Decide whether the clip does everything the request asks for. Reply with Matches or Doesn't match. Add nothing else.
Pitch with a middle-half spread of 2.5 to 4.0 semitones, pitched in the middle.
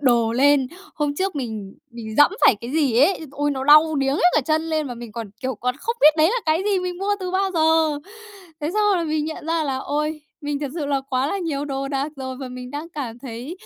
Doesn't match